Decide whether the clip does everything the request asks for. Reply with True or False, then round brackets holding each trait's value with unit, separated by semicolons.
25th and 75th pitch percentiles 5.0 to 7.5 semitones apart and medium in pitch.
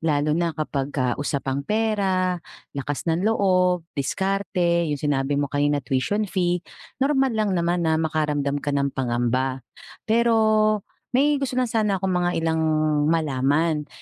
True (5.6 semitones; 165 Hz)